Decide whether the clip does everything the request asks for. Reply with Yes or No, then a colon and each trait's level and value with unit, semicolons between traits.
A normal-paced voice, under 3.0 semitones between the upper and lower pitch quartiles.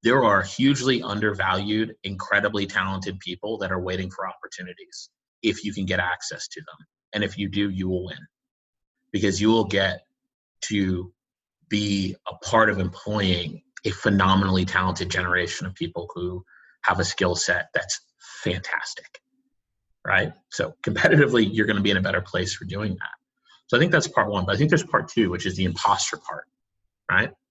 Yes: average, 175 wpm; narrow, 2.4 semitones